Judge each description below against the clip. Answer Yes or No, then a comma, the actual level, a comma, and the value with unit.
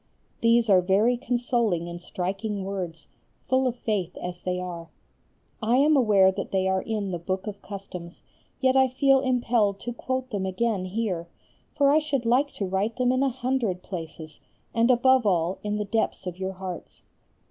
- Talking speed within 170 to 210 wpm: Yes, average, 180 wpm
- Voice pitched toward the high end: Yes, high, 210 Hz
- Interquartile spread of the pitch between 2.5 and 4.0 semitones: No, average, 5.0 semitones